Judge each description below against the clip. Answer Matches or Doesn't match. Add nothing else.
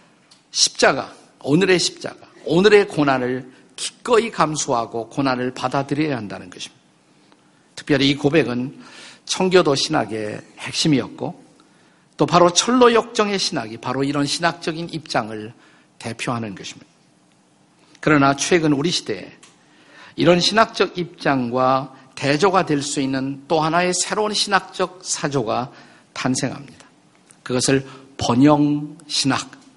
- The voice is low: Doesn't match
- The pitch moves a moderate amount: Matches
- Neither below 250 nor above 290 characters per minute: Matches